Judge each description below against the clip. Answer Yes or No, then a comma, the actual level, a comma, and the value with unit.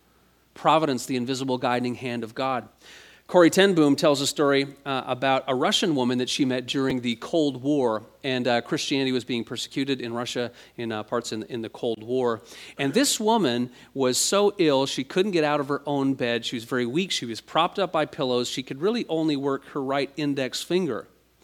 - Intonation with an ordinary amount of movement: Yes, average, 3.2 semitones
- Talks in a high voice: No, low, 135 Hz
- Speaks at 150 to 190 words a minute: No, fast, 205 wpm